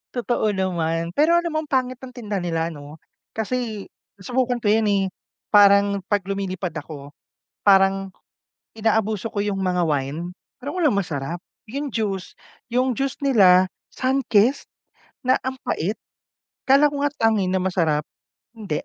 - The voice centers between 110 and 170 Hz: No, high, 200 Hz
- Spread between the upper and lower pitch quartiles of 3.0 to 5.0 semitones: No, wide, 5.5 semitones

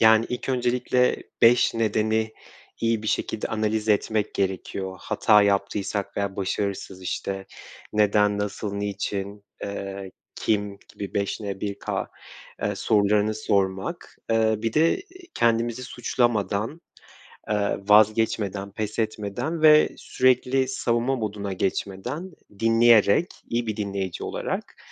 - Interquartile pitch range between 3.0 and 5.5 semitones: No, narrow, 2.4 semitones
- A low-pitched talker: Yes, low, 105 Hz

